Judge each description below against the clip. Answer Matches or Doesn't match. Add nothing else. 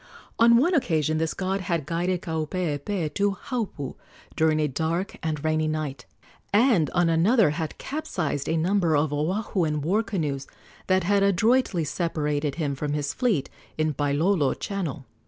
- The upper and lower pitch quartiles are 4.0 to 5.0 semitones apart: Matches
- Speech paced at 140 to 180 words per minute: Matches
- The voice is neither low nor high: Matches